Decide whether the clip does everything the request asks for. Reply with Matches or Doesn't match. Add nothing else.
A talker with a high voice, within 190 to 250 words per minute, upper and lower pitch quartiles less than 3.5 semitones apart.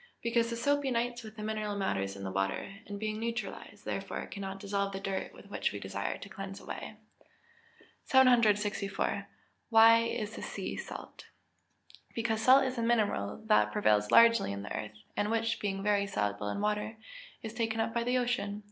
Doesn't match